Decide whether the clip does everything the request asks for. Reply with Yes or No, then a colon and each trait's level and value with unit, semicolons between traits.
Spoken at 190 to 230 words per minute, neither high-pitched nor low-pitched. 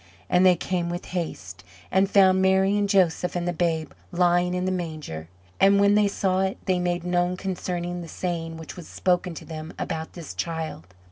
Yes: average, 195 wpm; medium, 175 Hz